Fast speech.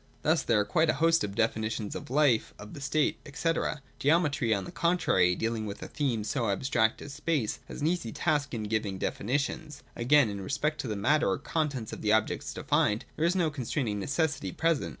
Yes: fast, 210 wpm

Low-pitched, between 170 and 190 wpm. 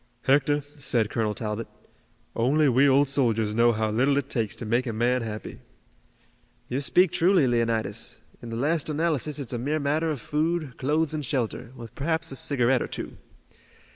Yes: low, 130 Hz; average, 175 wpm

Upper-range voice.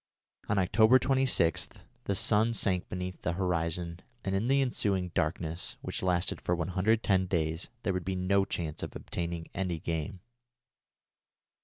No: very low, 90 Hz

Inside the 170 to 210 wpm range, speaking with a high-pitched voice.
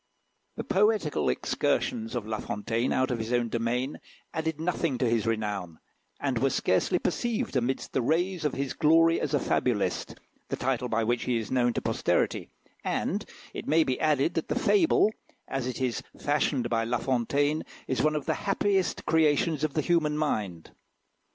No: average, 175 wpm; low, 135 Hz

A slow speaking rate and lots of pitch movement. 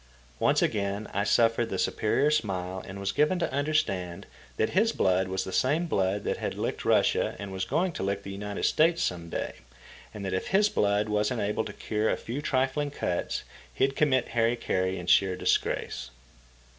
No: average, 190 wpm; wide, 6.3 semitones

